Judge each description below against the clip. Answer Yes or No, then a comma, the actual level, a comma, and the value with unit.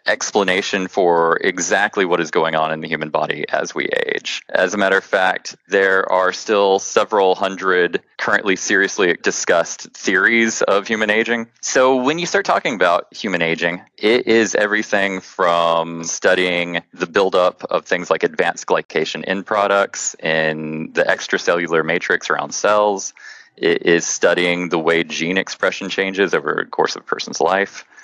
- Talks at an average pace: Yes, average, 160 wpm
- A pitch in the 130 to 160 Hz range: No, very low, 95 Hz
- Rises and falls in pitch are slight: No, average, 3.2 semitones